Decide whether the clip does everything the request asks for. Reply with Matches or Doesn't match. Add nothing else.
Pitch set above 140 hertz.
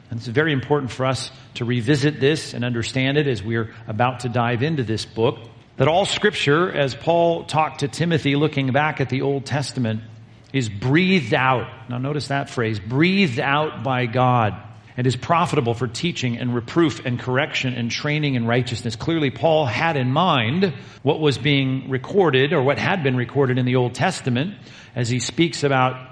Doesn't match